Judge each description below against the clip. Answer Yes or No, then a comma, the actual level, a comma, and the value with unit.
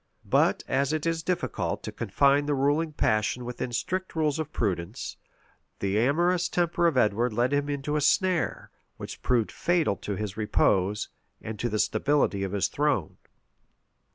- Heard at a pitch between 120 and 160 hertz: Yes, medium, 140 Hz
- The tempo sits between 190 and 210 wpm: No, average, 160 wpm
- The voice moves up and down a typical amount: No, wide, 6.4 semitones